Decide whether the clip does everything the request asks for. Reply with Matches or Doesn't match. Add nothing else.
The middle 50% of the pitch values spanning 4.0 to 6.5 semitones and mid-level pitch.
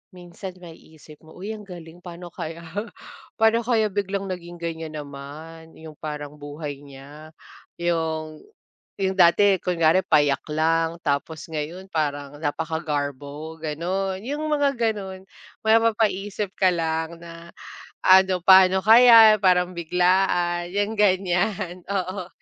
Doesn't match